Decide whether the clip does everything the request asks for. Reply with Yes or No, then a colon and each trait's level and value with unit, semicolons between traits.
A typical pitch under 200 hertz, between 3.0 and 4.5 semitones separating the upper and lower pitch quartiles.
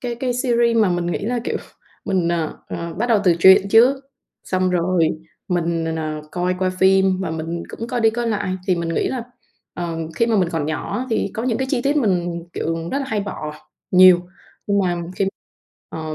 No: medium, 185 Hz; average, 5.2 semitones